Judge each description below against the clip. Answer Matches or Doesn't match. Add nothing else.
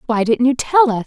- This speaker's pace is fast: Matches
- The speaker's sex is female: Matches